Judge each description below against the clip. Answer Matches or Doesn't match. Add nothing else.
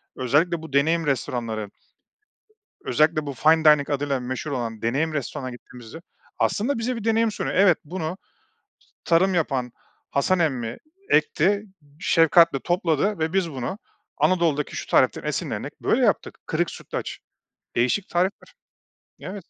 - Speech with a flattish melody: Doesn't match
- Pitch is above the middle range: Doesn't match